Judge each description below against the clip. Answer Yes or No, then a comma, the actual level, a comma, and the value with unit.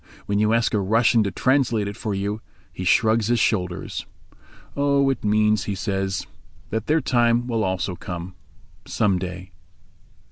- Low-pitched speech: Yes, low, 105 Hz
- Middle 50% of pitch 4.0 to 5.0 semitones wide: No, average, 3.3 semitones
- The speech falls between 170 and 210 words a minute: No, average, 150 wpm